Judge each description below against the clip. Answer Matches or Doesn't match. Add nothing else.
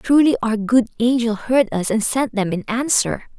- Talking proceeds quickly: Doesn't match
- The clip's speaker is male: Doesn't match